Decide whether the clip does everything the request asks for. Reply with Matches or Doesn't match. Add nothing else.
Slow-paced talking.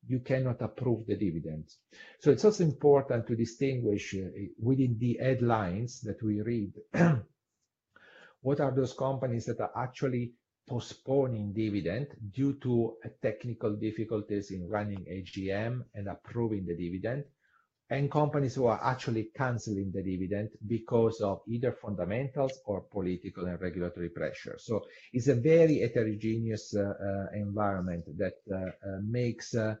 Doesn't match